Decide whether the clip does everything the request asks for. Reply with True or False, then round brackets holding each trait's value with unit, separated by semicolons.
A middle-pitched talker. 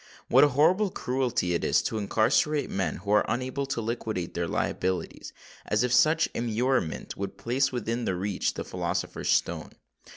False (120 Hz)